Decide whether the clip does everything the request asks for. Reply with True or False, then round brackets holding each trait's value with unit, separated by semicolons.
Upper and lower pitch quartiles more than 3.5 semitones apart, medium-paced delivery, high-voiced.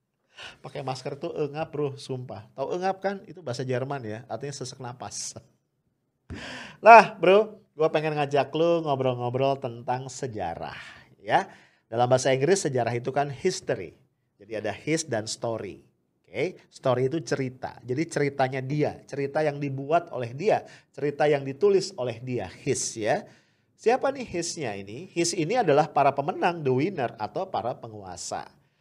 False (4.1 semitones; 150 wpm; 140 Hz)